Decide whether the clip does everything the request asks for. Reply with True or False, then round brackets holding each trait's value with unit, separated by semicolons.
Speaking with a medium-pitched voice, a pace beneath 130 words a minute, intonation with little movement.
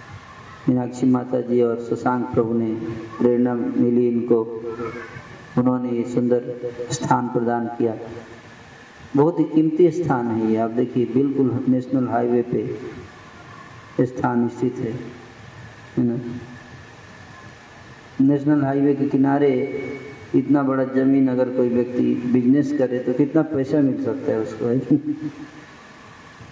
False (120 Hz; 115 wpm; 2.1 semitones)